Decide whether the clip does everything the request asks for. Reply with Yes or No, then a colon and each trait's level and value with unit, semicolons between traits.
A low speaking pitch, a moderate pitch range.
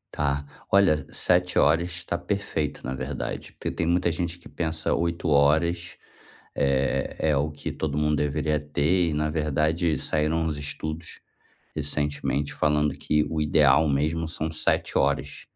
No: very low, 75 Hz; narrow, 2.3 semitones